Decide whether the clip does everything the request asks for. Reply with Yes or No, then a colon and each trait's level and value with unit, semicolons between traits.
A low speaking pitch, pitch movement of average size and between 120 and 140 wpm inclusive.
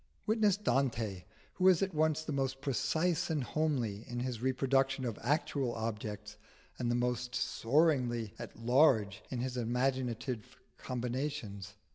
Yes: low, 125 Hz; average, 4.0 semitones; slow, 135 wpm